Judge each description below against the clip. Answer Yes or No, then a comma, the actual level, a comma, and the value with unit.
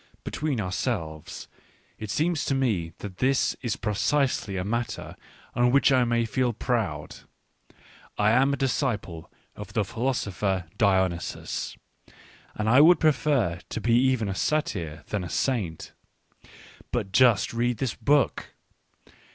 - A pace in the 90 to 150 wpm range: Yes, slow, 135 wpm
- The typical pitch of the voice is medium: No, low, 115 Hz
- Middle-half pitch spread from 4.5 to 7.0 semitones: Yes, average, 5.2 semitones